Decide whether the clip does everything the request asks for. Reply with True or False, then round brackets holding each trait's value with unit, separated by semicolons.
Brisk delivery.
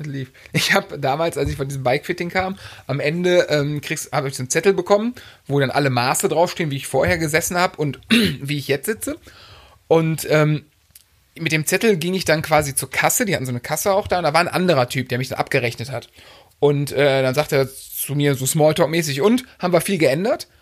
True (225 wpm)